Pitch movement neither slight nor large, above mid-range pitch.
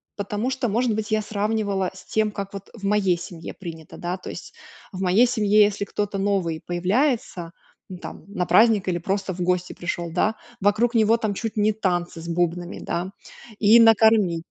Yes: average, 3.4 semitones; high, 200 Hz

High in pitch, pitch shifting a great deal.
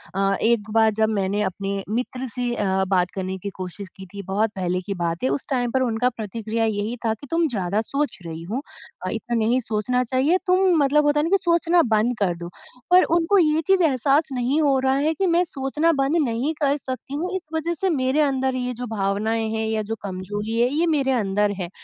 Yes: high, 235 Hz; wide, 5.8 semitones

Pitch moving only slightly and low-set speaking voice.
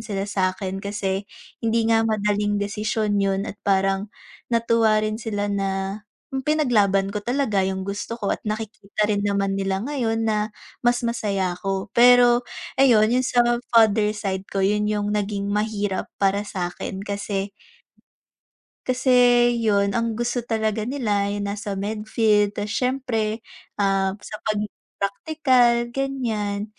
No: narrow, 2.3 semitones; high, 210 Hz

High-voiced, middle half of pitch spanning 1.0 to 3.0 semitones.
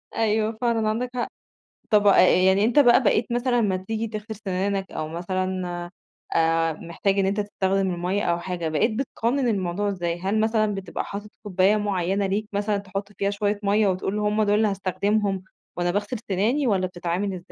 Yes: high, 200 Hz; narrow, 2.5 semitones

